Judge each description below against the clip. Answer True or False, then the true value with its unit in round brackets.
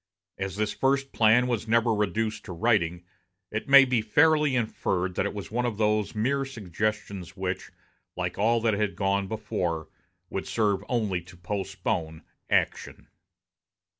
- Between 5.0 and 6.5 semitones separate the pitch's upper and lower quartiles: False (3.5 semitones)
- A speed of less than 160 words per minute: True (150 wpm)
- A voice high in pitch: False (105 Hz)